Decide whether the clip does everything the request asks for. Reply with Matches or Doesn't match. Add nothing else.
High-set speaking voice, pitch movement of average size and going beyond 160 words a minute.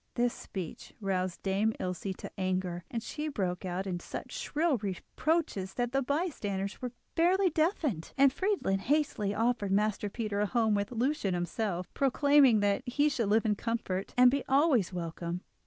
Doesn't match